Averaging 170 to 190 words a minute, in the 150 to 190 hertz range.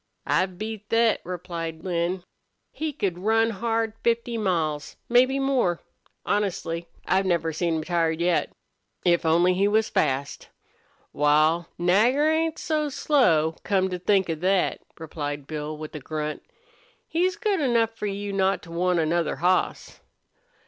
No: average, 145 wpm; medium, 185 Hz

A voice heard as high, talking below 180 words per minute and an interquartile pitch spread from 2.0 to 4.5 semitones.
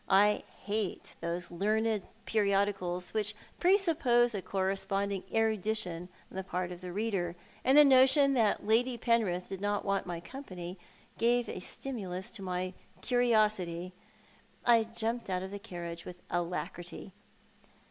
Yes: high, 200 Hz; slow, 135 wpm; average, 4.0 semitones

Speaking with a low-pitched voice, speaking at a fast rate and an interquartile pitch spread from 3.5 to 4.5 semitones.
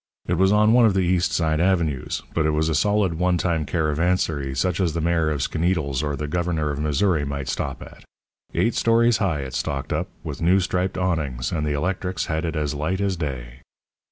Yes: very low, 80 Hz; fast, 210 wpm; average, 3.8 semitones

